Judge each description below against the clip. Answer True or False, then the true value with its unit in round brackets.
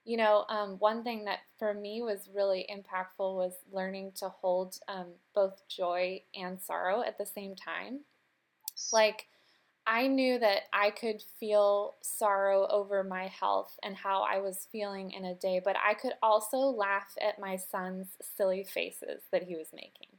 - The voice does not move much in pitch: True (2.0 semitones)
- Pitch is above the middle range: True (200 Hz)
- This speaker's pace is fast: False (170 wpm)